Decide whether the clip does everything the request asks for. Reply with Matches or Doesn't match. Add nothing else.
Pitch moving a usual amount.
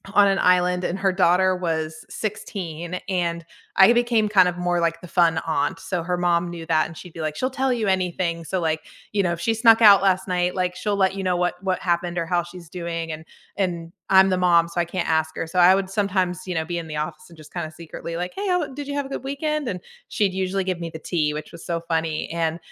Doesn't match